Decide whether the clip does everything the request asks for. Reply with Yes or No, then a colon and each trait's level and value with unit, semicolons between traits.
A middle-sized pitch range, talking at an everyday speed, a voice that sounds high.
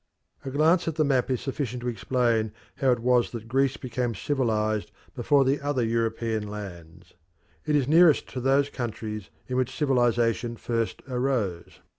No: average, 3.2 semitones; average, 160 wpm; low, 125 Hz